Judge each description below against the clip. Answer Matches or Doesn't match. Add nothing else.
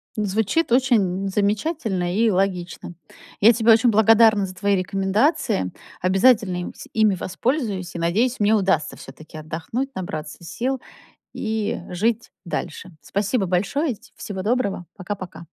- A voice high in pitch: Matches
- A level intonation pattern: Doesn't match